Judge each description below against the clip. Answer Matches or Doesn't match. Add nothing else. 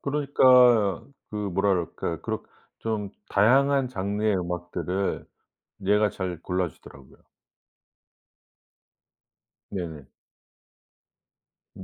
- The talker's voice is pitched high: Doesn't match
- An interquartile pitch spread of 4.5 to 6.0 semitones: Doesn't match